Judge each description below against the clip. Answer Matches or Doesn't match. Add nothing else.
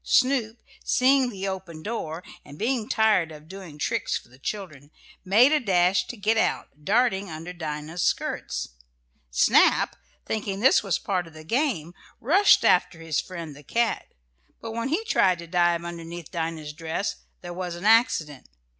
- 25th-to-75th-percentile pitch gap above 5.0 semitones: Matches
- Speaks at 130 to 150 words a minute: Doesn't match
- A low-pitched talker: Doesn't match